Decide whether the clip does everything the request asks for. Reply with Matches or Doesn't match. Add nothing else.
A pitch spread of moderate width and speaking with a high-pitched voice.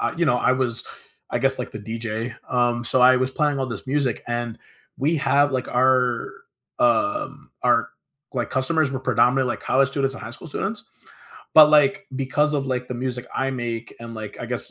Doesn't match